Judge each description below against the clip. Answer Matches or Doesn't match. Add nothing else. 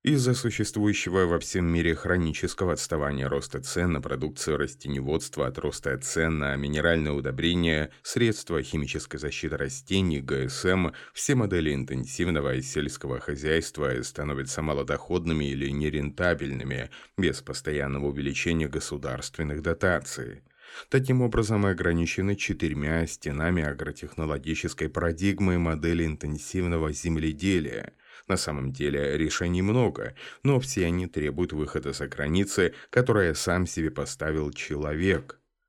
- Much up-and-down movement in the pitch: Doesn't match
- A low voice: Matches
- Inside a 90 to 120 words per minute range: Matches